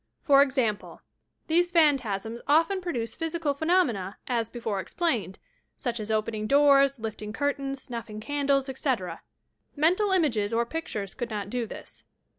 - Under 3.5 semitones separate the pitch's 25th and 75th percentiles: No, average, 5.3 semitones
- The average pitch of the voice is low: No, very high, 260 Hz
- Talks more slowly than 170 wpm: Yes, average, 140 wpm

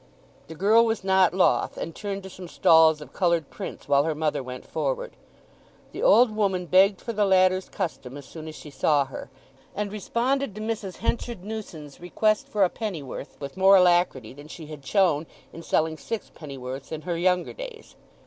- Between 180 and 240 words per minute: Yes, average, 185 wpm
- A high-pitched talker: No, medium, 180 Hz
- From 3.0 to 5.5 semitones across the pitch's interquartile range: Yes, average, 5.2 semitones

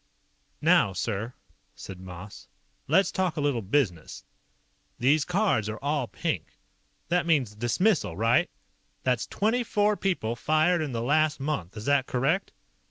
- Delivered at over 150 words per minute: No, average, 140 wpm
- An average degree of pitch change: No, wide, 7.1 semitones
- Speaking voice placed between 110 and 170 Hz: Yes, low, 135 Hz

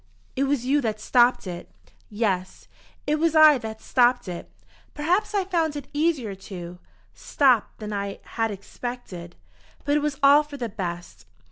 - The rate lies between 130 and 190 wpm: Yes, average, 160 wpm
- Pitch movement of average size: No, wide, 6.7 semitones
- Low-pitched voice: No, high, 245 Hz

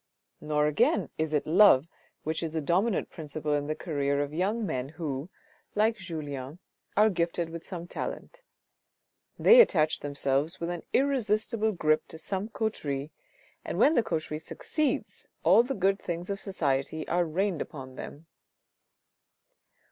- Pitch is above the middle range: No, medium, 165 Hz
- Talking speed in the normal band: Yes, average, 150 wpm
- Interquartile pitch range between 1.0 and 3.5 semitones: No, average, 4.9 semitones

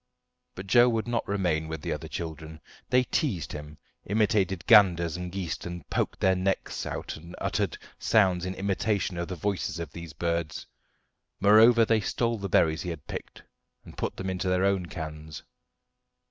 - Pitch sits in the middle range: No, very low, 90 Hz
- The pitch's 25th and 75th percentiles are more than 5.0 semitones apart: No, average, 3.5 semitones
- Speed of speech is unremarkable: Yes, average, 175 wpm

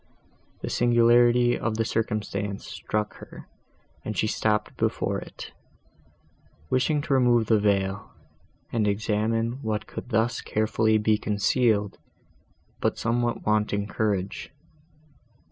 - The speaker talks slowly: Yes, slow, 110 wpm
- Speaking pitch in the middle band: No, low, 110 Hz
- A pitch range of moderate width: No, narrow, 2.1 semitones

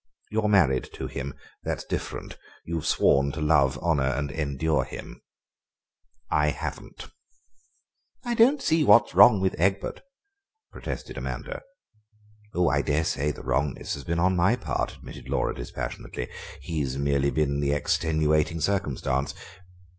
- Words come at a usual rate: No, slow, 130 wpm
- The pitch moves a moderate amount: Yes, average, 4.2 semitones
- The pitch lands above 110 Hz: No, very low, 75 Hz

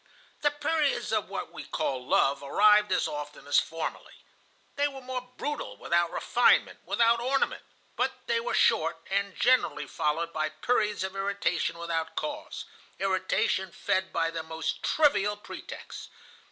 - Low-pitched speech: No, high, 195 Hz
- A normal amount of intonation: No, wide, 7.4 semitones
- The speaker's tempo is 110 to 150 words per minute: Yes, average, 145 wpm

